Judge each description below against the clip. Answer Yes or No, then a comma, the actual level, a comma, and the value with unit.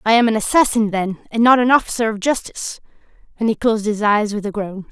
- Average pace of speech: No, fast, 230 wpm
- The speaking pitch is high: Yes, high, 220 Hz